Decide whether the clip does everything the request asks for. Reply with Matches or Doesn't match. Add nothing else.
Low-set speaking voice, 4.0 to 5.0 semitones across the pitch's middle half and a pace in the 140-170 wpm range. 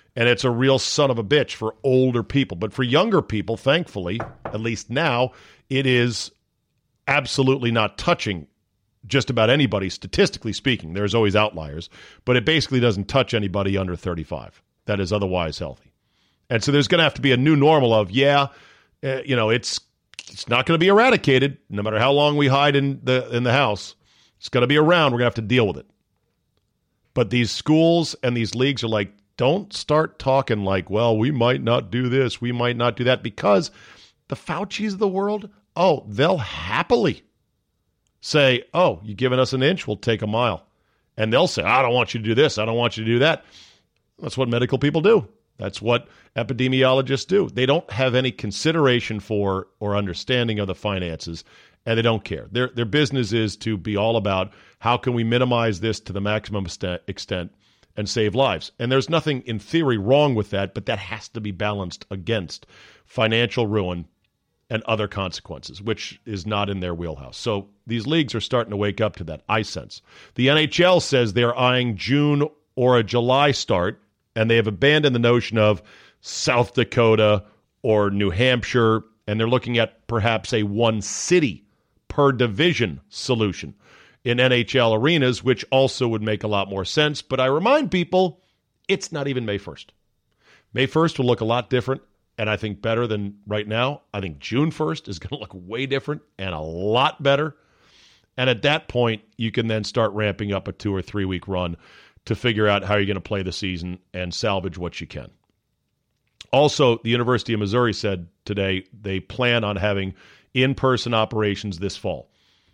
Doesn't match